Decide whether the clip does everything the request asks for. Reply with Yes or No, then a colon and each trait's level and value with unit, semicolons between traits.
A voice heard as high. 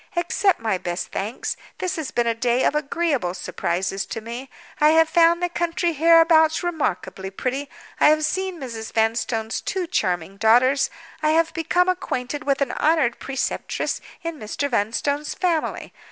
Yes: very high, 285 Hz